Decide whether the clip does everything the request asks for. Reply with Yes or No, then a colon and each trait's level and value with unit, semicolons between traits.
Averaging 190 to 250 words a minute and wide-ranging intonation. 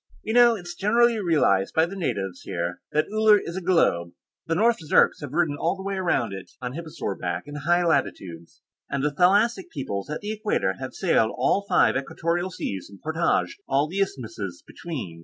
Yes: average, 200 wpm; wide, 8.4 semitones